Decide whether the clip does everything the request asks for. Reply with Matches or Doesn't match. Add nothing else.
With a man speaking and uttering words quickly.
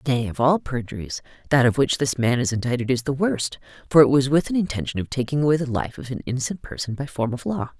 Doesn't match